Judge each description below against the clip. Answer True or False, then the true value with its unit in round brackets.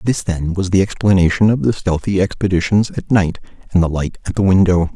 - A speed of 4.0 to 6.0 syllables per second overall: True (5.6 syllables/s)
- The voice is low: True (95 Hz)